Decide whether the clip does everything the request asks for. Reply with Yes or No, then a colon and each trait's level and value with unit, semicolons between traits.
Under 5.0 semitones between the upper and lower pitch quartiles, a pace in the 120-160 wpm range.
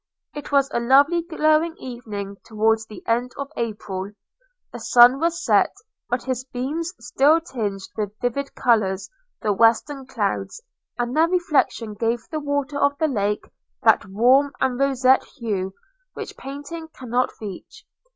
Yes: average, 4.5 semitones; average, 150 wpm